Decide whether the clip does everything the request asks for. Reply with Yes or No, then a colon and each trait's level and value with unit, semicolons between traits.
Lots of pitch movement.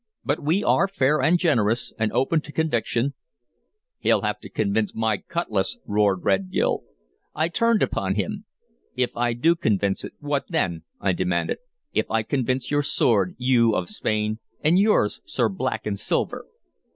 Yes: wide, 6.2 semitones